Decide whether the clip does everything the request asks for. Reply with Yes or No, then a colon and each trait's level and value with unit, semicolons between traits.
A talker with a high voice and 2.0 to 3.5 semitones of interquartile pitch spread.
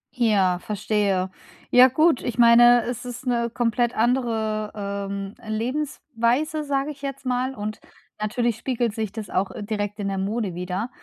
Yes: high, 230 Hz; average, 3.2 semitones